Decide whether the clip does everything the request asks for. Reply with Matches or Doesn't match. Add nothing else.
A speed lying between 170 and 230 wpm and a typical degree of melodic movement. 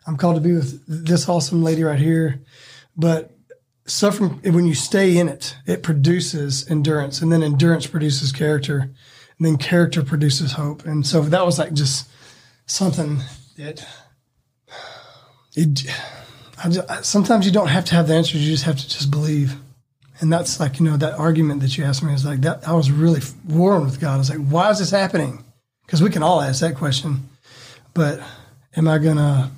Matches